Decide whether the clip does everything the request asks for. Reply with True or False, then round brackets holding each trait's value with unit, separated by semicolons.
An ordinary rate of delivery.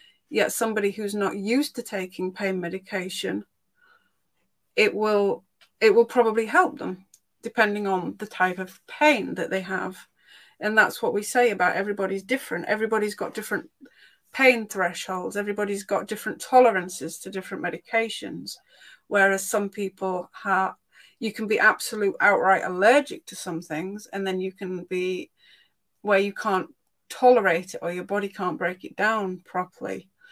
True (150 wpm)